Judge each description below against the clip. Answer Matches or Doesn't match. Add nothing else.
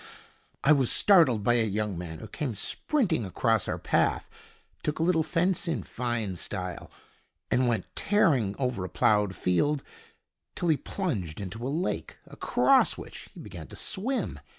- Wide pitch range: Matches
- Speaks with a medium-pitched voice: Doesn't match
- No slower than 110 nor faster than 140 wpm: Doesn't match